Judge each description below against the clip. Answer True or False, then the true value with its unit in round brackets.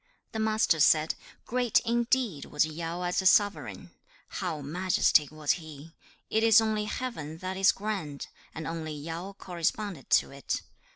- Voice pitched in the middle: True (175 Hz)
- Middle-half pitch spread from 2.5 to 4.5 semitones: False (5.5 semitones)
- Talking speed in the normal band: True (150 wpm)